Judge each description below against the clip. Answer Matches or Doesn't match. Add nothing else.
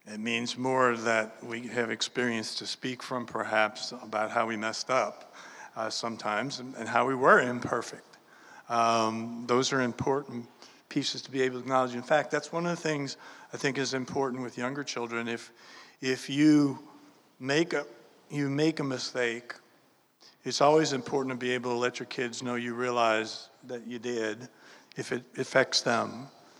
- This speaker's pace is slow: Doesn't match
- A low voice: Matches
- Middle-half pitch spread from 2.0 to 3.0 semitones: Matches